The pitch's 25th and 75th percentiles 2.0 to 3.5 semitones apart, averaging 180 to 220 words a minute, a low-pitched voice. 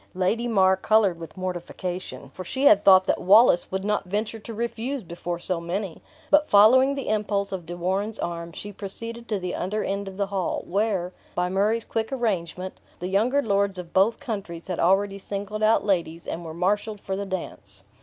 No: average, 3.0 semitones; average, 195 wpm; high, 195 Hz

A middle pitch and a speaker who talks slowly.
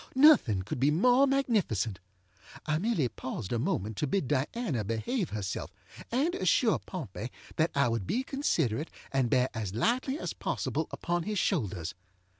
No: medium, 150 Hz; average, 155 wpm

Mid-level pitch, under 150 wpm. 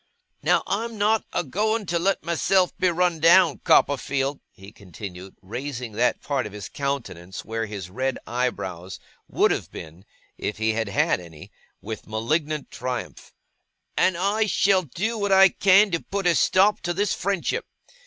No: medium, 145 Hz; average, 165 wpm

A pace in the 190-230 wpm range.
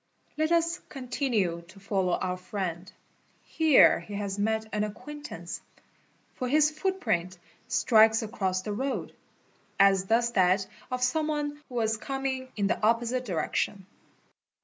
No: average, 145 wpm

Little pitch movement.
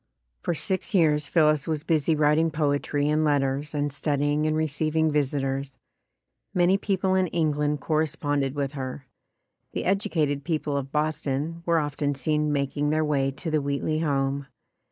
Yes: narrow, 1.9 semitones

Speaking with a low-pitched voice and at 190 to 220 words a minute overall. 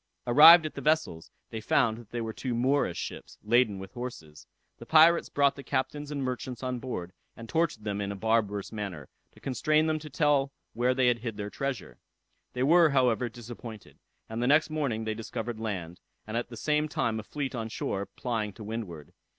Yes: low, 120 Hz; average, 200 wpm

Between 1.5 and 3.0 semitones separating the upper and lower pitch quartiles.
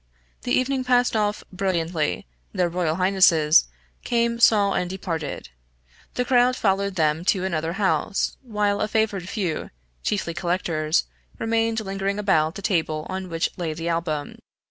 No: average, 4.3 semitones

